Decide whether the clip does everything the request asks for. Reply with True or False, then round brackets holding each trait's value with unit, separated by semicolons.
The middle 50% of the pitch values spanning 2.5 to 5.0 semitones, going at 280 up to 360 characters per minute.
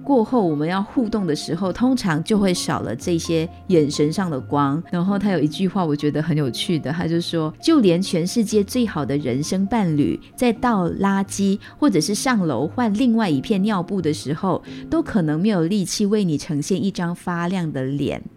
False (5.4 semitones; 290 characters per minute)